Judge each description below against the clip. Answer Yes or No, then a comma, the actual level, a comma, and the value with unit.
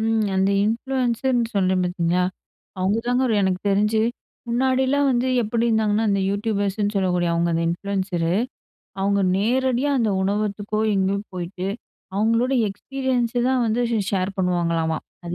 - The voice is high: Yes, high, 205 Hz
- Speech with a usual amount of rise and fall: Yes, average, 4.1 semitones